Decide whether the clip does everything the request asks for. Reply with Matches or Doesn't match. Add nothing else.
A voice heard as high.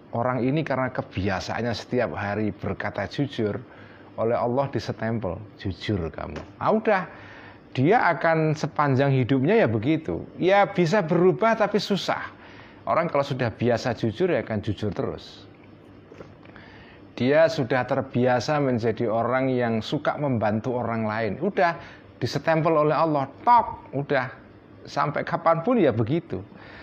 Doesn't match